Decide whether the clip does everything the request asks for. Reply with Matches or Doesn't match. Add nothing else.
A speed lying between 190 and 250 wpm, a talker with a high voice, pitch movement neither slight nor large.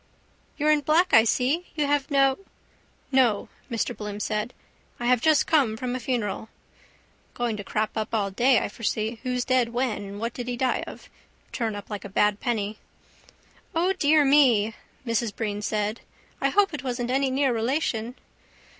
Doesn't match